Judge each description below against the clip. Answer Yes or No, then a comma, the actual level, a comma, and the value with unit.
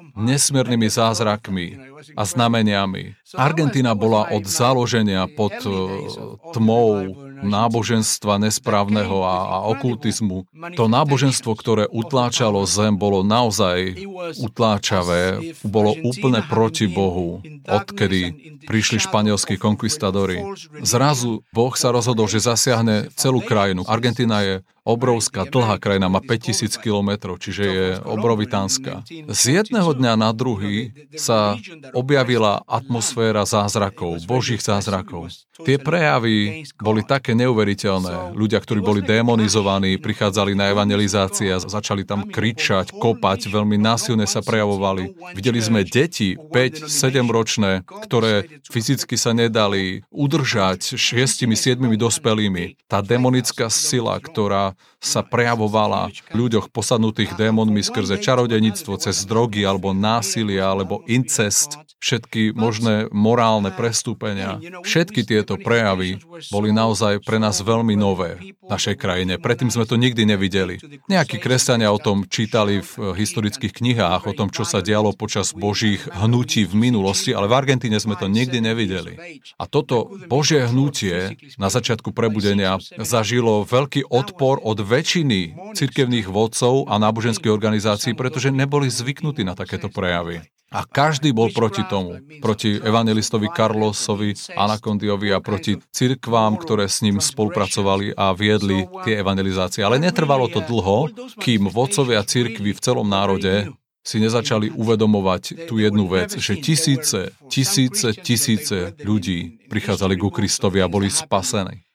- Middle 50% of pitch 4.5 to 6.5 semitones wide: No, average, 3.3 semitones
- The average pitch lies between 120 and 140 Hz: No, low, 110 Hz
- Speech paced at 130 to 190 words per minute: No, average, 120 wpm